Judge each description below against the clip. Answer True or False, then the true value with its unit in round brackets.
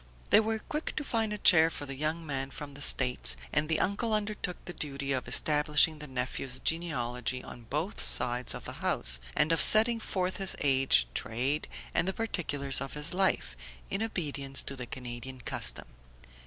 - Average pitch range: False (5.9 semitones)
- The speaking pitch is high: False (150 Hz)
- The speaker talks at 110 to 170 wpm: False (180 wpm)